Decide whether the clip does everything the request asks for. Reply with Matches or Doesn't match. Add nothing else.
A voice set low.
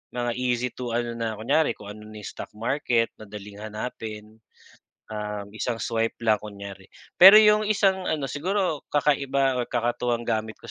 Matches